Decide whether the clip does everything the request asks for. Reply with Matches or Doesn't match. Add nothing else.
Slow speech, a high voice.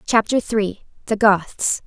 Matches